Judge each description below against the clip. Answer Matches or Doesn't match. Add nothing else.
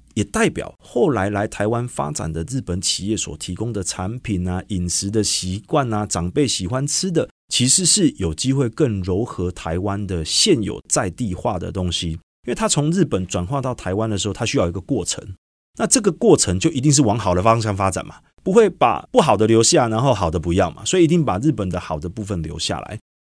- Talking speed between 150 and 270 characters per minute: Doesn't match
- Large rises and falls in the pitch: Matches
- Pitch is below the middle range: Matches